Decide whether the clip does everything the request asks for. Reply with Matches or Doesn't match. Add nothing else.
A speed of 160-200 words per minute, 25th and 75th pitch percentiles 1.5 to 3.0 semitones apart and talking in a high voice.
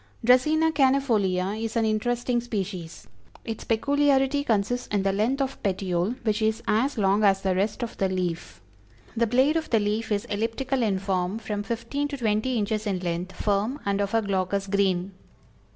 Doesn't match